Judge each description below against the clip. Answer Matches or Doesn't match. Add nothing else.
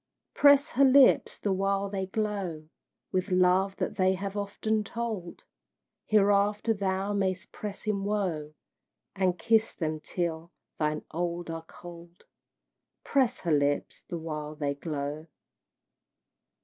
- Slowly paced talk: Matches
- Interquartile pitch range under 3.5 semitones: Doesn't match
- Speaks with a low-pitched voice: Doesn't match